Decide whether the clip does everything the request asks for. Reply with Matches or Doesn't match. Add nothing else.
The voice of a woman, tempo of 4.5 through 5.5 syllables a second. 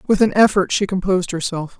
Doesn't match